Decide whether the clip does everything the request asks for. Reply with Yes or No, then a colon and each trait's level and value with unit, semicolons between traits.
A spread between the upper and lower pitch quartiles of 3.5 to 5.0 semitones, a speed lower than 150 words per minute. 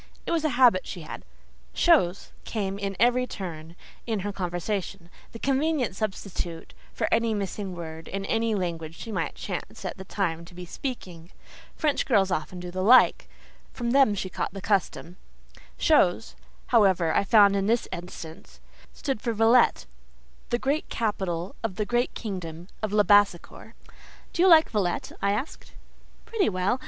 No: average, 4.7 semitones; average, 160 wpm